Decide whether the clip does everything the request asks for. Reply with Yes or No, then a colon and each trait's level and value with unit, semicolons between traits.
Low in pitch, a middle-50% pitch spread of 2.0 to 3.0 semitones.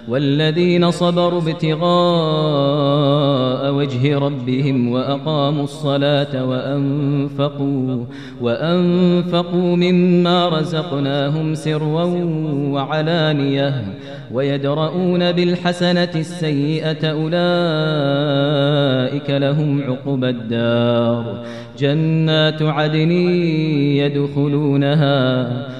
No: medium, 145 Hz; narrow, 2.4 semitones